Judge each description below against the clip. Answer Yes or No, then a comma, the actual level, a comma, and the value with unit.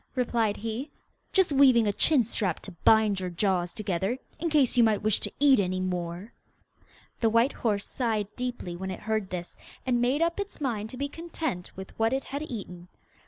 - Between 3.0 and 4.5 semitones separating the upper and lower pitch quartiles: No, wide, 5.4 semitones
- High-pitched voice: Yes, high, 220 Hz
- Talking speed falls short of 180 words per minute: No, average, 195 wpm